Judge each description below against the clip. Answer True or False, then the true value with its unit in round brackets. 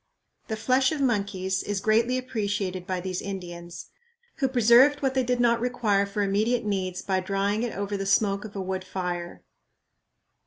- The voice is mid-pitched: False (205 Hz)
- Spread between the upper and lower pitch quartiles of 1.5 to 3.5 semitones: False (3.9 semitones)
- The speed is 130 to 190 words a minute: True (170 wpm)